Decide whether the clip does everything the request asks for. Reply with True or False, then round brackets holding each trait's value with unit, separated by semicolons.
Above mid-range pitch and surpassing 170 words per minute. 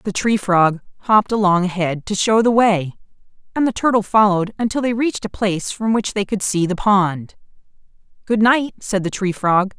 True (200 Hz; 195 wpm)